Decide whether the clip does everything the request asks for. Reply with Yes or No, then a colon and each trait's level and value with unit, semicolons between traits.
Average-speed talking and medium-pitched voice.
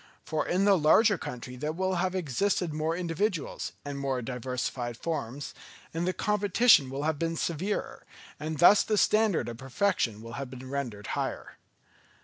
Yes: average, 160 wpm; medium, 155 Hz